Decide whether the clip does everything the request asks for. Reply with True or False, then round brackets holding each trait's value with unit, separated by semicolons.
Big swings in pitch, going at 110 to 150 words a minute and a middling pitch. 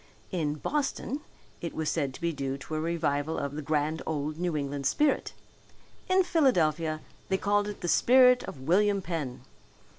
False (5.7 semitones; 170 wpm; 160 Hz)